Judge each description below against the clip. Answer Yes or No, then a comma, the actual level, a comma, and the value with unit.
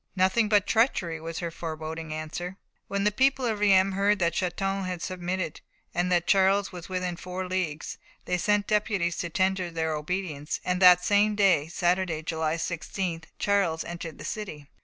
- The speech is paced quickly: No, average, 170 wpm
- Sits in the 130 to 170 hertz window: No, medium, 180 Hz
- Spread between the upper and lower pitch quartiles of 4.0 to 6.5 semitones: No, average, 2.9 semitones